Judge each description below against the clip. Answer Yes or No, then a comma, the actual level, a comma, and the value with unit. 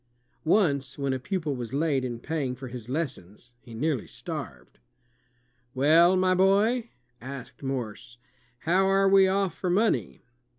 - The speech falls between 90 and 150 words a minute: Yes, average, 140 wpm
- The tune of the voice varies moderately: No, wide, 6.8 semitones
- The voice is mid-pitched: Yes, medium, 145 Hz